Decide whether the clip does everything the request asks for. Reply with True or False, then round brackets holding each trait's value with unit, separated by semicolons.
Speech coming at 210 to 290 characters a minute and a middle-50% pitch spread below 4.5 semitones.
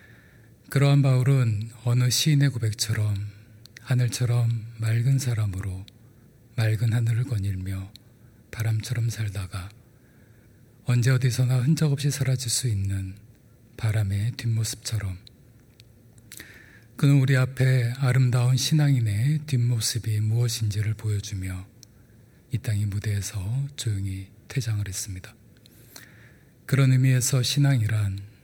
True (250 characters per minute; 2.7 semitones)